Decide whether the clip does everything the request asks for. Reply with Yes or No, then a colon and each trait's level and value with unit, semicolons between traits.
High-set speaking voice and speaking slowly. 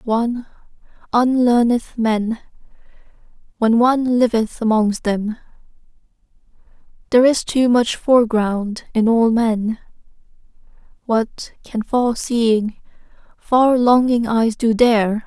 Yes: high, 230 Hz; slow, 95 wpm